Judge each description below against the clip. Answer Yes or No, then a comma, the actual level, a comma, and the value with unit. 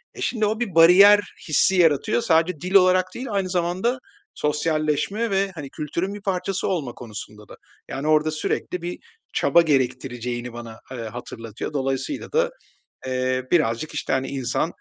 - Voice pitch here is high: No, medium, 155 Hz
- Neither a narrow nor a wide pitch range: No, wide, 6.6 semitones